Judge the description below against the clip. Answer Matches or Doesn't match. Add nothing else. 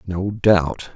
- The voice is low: Matches